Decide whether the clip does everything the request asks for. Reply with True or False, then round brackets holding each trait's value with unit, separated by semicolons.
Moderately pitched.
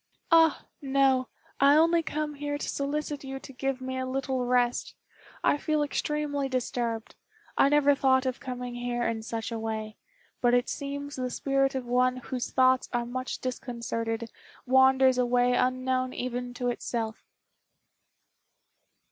False (255 Hz)